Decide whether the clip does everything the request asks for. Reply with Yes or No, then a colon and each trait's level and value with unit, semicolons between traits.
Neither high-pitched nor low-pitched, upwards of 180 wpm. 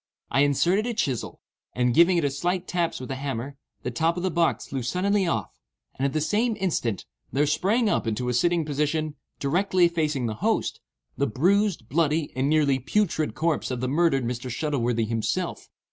Yes: medium, 150 Hz; average, 190 wpm